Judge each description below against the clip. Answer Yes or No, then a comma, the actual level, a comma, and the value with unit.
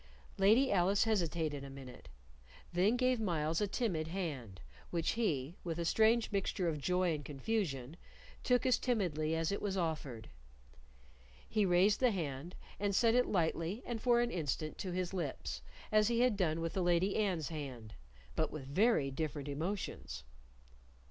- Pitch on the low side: No, medium, 175 Hz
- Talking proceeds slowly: No, average, 160 wpm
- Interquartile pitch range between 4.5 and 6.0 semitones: Yes, average, 5.3 semitones